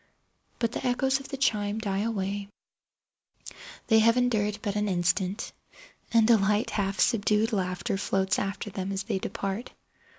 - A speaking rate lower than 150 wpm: Yes, average, 140 wpm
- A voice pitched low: No, high, 205 Hz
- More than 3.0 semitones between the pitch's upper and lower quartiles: No, average, 2.7 semitones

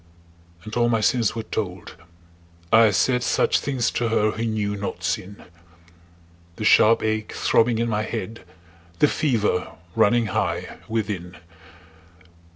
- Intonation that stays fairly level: Yes, narrow, 1.9 semitones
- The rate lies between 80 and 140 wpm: Yes, slow, 135 wpm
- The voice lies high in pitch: No, low, 110 Hz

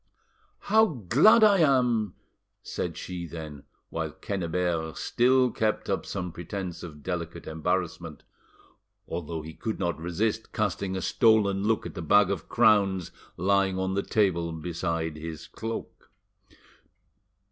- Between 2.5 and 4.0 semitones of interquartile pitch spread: No, average, 4.5 semitones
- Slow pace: Yes, slow, 130 wpm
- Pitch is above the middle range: No, very low, 95 Hz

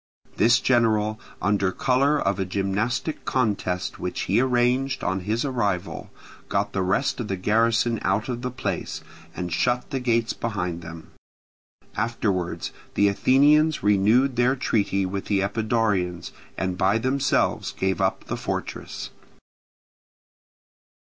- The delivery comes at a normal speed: No, slow, 130 wpm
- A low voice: Yes, low, 110 Hz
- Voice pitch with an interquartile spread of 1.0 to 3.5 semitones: No, average, 4.4 semitones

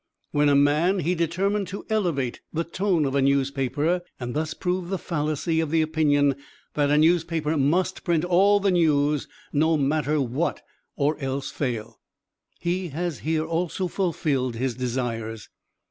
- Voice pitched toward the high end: No, medium, 155 Hz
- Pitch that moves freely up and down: No, average, 3.8 semitones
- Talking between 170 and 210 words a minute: No, average, 155 wpm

